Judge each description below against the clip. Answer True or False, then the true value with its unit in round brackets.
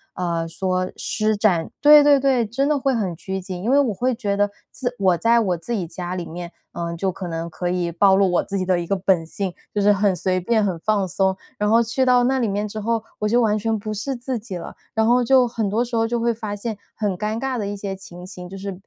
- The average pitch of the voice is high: True (205 Hz)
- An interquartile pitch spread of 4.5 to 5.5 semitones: False (4.0 semitones)